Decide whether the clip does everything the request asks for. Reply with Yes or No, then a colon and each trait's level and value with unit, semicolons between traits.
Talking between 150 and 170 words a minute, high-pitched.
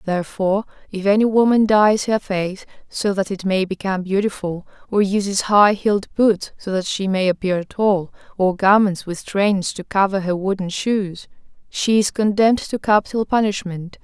Yes: average, 165 wpm; high, 200 Hz